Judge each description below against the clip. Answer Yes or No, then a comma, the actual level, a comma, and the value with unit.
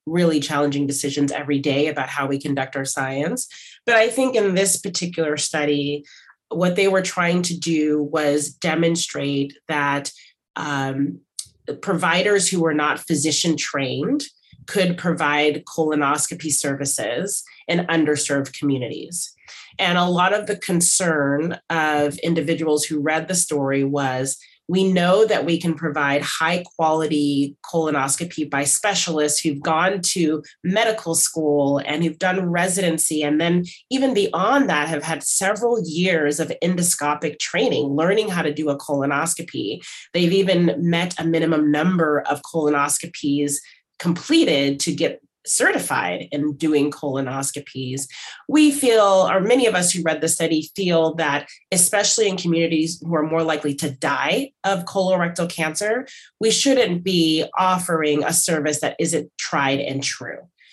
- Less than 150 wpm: Yes, average, 140 wpm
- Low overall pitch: No, medium, 160 Hz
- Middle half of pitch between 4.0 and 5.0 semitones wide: No, average, 3.5 semitones